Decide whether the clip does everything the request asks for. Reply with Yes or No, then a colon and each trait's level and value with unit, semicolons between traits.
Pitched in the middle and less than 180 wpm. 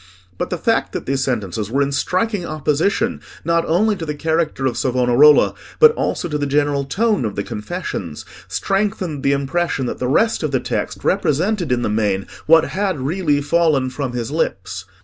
No: medium, 145 Hz; average, 185 wpm